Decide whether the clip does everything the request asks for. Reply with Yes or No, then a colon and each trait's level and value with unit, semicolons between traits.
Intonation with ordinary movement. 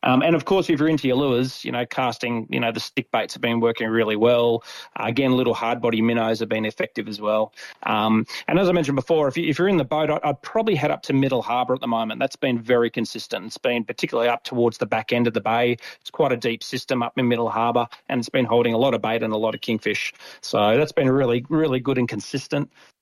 Yes: average, 3.0 semitones